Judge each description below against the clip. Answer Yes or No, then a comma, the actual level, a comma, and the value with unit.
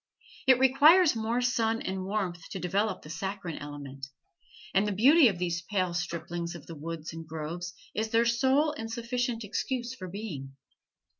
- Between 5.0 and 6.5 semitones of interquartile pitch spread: Yes, wide, 5.6 semitones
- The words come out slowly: No, average, 165 wpm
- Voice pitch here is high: Yes, high, 195 Hz